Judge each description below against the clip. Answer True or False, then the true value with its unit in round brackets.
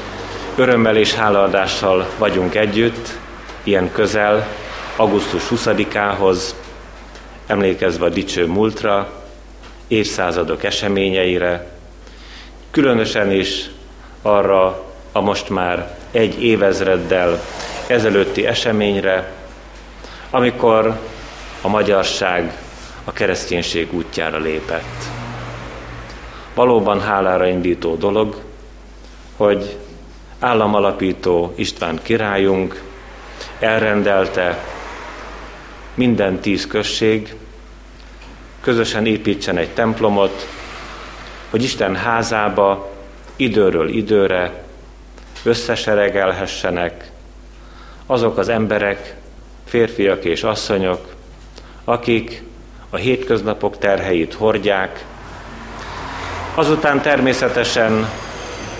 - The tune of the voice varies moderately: True (3.4 semitones)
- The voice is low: True (100 Hz)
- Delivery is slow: True (70 wpm)